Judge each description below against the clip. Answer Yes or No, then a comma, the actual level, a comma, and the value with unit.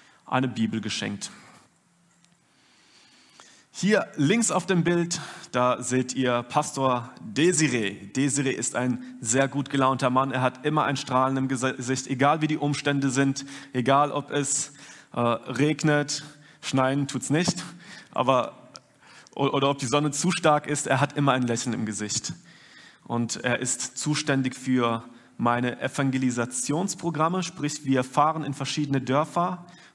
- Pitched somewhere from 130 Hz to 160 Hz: Yes, medium, 140 Hz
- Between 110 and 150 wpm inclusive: Yes, average, 140 wpm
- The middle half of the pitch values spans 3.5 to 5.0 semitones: No, average, 2.7 semitones